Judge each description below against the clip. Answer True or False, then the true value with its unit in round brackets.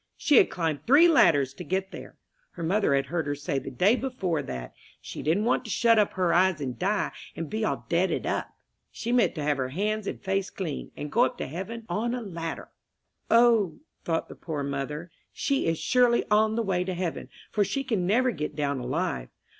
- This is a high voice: False (180 Hz)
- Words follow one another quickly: True (215 wpm)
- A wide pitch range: True (6.7 semitones)